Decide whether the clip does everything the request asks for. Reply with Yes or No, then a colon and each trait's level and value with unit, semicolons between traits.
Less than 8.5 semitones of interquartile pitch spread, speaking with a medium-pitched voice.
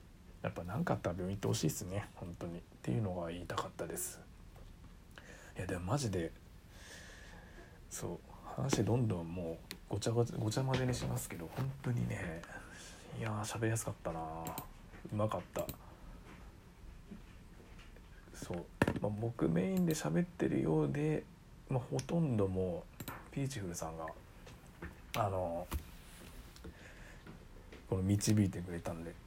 No: wide, 5.5 semitones; very low, 95 Hz